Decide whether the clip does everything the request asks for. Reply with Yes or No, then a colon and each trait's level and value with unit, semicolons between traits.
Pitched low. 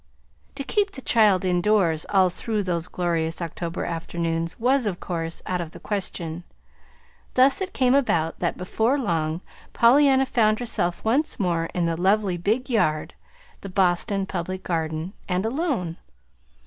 No: medium, 185 Hz